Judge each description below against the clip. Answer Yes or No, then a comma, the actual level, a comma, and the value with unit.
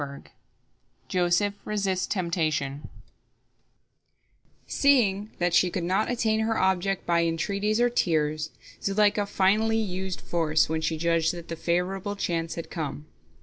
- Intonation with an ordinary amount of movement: Yes, average, 3.5 semitones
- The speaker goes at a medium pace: No, slow, 130 wpm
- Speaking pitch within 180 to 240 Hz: Yes, medium, 185 Hz